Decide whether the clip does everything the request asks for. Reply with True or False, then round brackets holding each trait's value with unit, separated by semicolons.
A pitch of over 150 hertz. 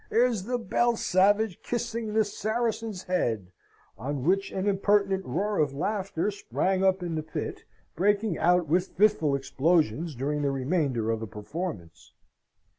True (185 Hz)